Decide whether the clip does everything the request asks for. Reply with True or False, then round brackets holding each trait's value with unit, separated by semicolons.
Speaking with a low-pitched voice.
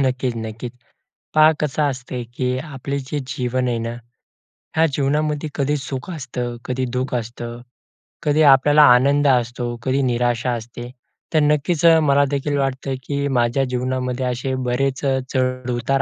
True (130 Hz)